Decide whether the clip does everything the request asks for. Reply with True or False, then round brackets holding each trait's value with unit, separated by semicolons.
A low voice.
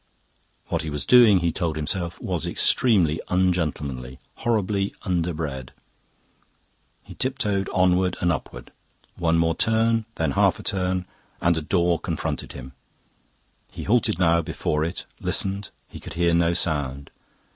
True (85 Hz)